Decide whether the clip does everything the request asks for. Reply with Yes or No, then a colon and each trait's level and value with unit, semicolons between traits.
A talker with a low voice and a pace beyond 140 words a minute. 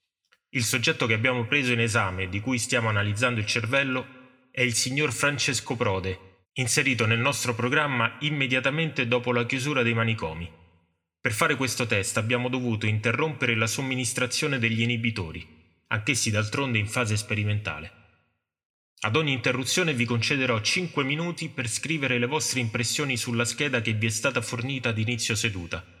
Yes: low, 120 Hz; average, 150 wpm